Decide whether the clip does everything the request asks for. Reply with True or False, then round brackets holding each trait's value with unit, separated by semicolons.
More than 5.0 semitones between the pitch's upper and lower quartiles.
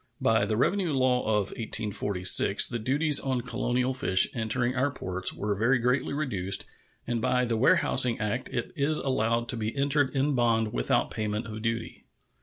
False (3.2 semitones)